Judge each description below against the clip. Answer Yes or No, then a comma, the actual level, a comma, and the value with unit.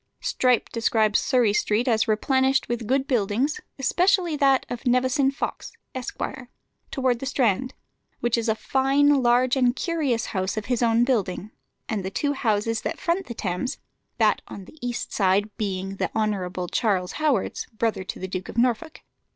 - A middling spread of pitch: Yes, average, 4.0 semitones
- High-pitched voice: Yes, high, 240 Hz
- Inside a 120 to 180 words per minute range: Yes, average, 165 wpm